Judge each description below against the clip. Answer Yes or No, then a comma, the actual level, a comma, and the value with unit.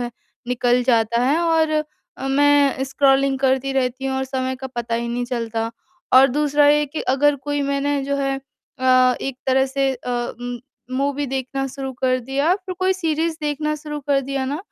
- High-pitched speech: Yes, very high, 270 Hz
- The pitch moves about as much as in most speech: No, narrow, 2.0 semitones